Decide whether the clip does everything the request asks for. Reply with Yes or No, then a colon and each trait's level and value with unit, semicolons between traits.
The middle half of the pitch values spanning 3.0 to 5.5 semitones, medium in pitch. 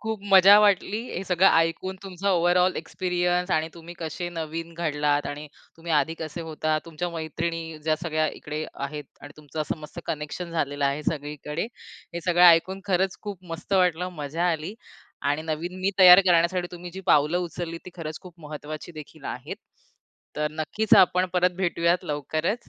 No: narrow, 2.6 semitones; medium, 170 Hz